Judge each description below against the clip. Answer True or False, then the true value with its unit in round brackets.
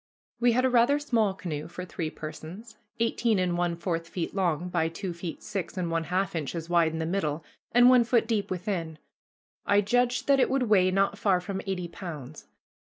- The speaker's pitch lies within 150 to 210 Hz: True (185 Hz)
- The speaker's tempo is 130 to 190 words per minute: False (200 wpm)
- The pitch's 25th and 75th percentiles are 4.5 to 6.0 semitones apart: True (4.8 semitones)